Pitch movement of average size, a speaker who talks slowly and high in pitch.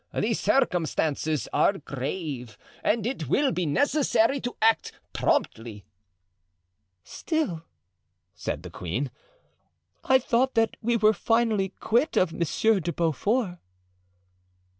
No: wide, 7.2 semitones; slow, 110 wpm; high, 195 Hz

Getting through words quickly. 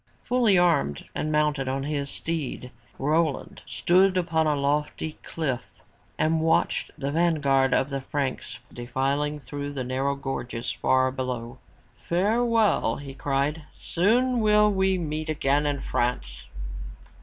No: slow, 135 wpm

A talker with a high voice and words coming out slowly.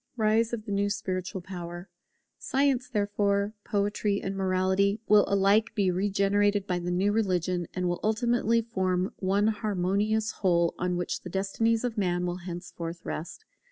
No: high, 200 Hz; average, 155 wpm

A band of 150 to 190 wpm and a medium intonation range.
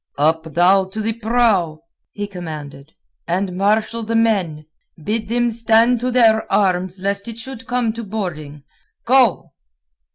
No: average, 140 wpm; average, 4.7 semitones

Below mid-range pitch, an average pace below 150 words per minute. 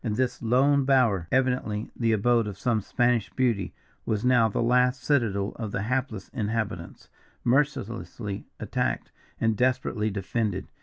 Yes: low, 115 Hz; average, 140 wpm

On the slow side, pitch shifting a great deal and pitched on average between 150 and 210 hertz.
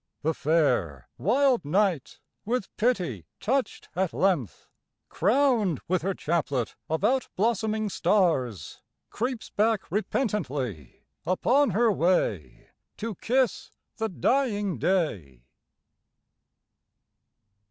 Yes: slow, 95 wpm; wide, 7.3 semitones; high, 190 Hz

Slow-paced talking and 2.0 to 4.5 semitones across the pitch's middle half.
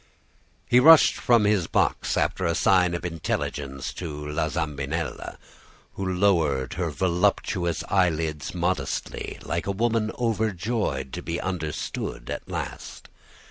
Yes: slow, 125 wpm; average, 4.2 semitones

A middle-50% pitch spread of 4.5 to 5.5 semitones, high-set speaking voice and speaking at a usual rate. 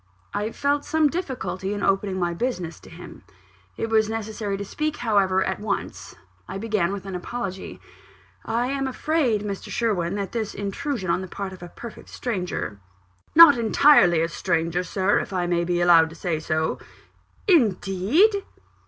Yes: average, 5.0 semitones; high, 200 Hz; average, 170 wpm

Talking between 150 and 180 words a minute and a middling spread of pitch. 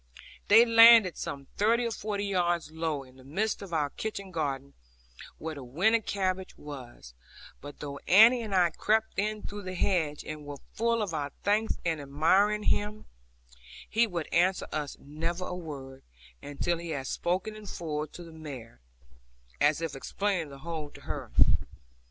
No: average, 170 wpm; wide, 5.8 semitones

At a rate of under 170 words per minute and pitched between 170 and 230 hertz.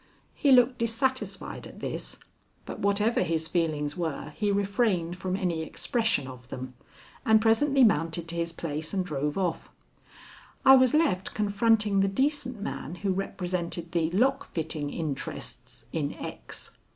Yes: average, 145 wpm; medium, 185 Hz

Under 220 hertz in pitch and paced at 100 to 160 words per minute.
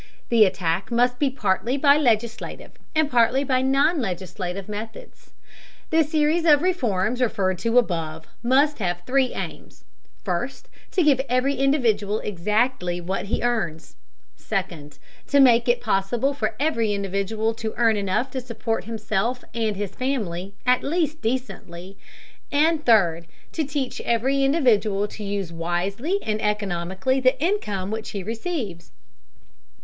No: high, 225 Hz; average, 140 wpm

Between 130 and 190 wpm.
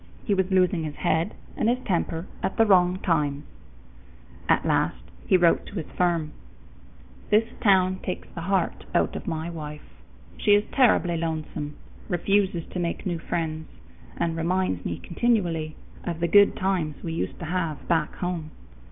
Yes: average, 160 wpm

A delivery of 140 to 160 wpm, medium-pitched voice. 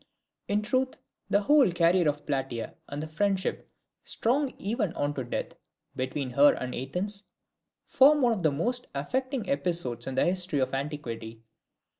Yes: average, 150 wpm; medium, 170 Hz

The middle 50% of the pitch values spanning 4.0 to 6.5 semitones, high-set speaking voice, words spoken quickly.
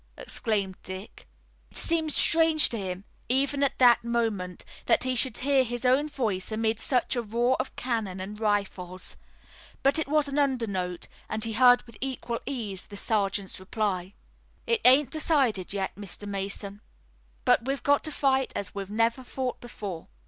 No: average, 4.9 semitones; high, 230 Hz; average, 165 wpm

